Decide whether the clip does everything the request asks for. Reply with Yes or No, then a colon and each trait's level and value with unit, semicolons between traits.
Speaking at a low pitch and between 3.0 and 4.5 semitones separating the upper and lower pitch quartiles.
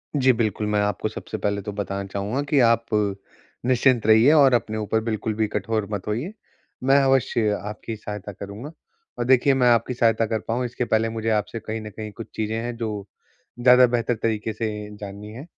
No: low, 110 Hz; narrow, 2.5 semitones